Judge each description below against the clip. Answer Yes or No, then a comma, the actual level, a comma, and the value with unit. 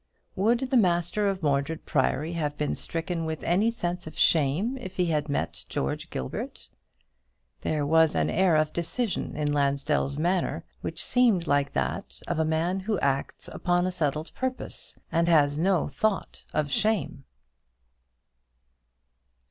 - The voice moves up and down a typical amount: Yes, average, 4.1 semitones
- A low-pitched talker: No, medium, 165 Hz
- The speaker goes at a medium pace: Yes, average, 150 wpm